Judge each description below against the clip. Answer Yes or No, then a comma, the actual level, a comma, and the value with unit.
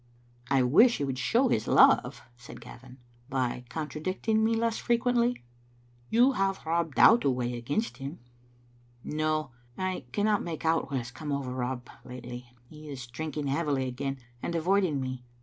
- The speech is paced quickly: No, average, 160 wpm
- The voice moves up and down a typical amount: No, wide, 6.8 semitones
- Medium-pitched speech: Yes, medium, 150 Hz